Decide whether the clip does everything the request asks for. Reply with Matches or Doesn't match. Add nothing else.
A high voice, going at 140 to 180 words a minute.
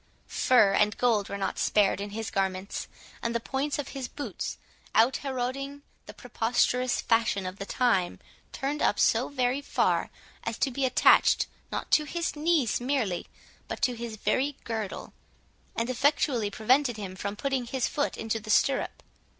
Matches